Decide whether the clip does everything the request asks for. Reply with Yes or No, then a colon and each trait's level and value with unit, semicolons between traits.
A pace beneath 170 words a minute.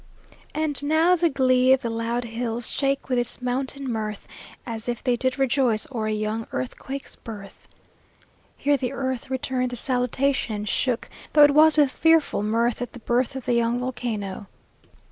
No: average, 175 wpm